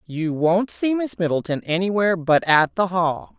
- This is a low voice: No, medium, 180 Hz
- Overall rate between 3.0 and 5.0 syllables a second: Yes, 4.7 syllables/s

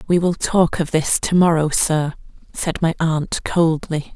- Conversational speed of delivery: Yes, average, 175 wpm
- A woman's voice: Yes, female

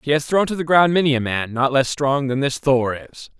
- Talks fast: Yes, fast, 285 wpm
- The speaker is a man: Yes, male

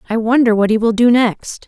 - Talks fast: Yes, fast, 250 wpm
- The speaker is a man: No, female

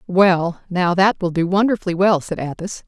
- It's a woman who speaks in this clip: Yes, female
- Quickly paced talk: No, average, 190 wpm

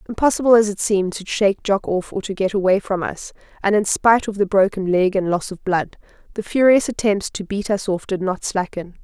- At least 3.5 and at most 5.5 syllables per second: No, 5.7 syllables/s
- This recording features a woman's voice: Yes, female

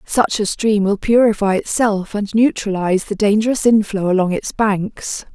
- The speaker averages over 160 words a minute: No, average, 155 wpm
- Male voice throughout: No, female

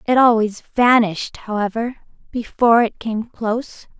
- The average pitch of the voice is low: No, high, 225 Hz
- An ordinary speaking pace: No, slow, 120 wpm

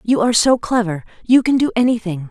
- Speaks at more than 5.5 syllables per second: Yes, 6.1 syllables/s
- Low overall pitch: No, high, 225 Hz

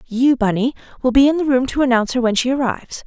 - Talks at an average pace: No, fast, 255 wpm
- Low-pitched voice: No, very high, 255 Hz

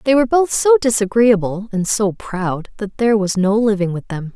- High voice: Yes, high, 215 Hz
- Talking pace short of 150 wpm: No, fast, 205 wpm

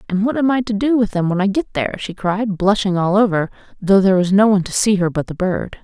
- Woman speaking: Yes, female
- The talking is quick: Yes, fast, 290 wpm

